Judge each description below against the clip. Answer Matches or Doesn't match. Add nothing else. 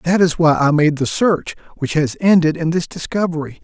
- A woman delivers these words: Doesn't match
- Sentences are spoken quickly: Matches